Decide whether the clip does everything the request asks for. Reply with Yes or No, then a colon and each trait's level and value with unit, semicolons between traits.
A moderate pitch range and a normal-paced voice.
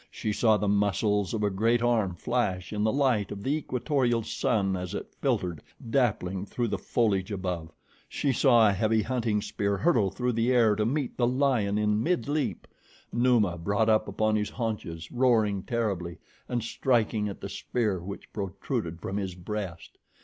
Yes: average, 3.5 semitones; average, 170 wpm